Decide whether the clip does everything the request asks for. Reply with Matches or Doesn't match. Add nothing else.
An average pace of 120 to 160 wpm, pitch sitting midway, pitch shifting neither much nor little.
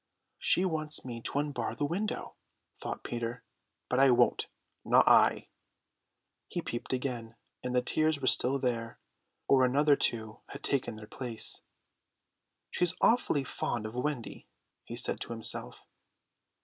Doesn't match